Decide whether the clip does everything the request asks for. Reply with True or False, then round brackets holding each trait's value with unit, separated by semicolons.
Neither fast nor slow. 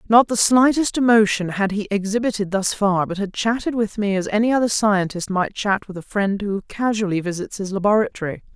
True (195 wpm)